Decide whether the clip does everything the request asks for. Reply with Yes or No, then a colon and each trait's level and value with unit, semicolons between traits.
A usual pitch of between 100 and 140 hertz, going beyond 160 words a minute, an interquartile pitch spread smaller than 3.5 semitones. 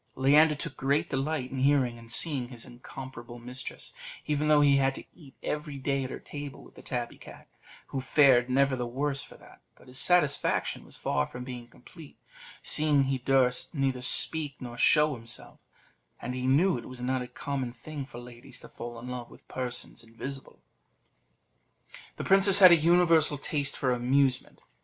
Yes: low, 135 Hz; average, 180 wpm; average, 2.9 semitones